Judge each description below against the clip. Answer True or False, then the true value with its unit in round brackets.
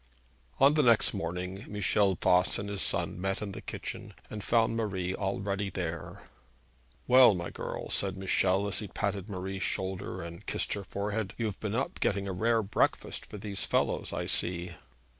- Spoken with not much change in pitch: True (2.2 semitones)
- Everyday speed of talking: True (175 wpm)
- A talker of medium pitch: False (100 Hz)